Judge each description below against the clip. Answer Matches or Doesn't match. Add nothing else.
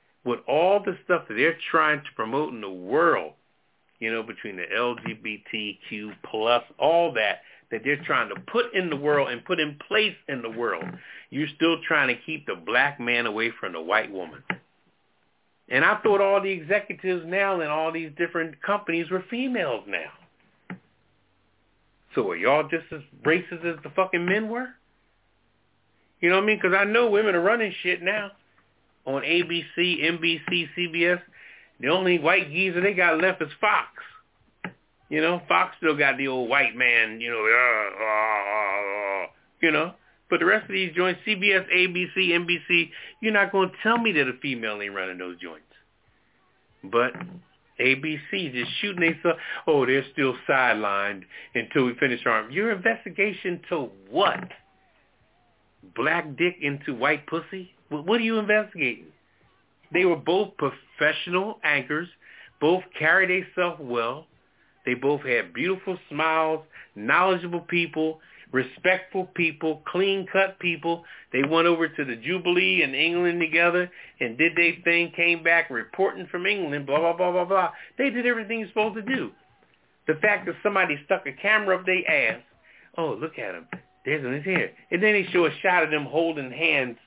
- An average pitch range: Matches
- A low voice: Doesn't match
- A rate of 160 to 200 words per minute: Matches